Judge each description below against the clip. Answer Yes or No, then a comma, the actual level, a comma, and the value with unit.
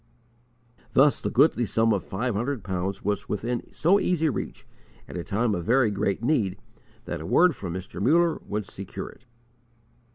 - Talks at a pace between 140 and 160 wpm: No, average, 170 wpm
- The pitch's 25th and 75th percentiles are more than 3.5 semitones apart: Yes, wide, 5.6 semitones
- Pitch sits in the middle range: No, low, 110 Hz